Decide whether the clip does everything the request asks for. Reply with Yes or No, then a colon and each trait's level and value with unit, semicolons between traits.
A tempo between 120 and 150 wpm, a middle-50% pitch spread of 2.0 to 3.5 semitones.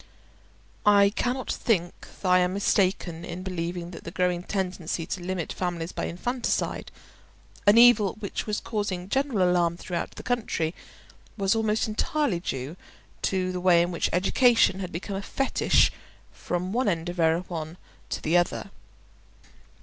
Yes: average, 140 wpm; average, 3.0 semitones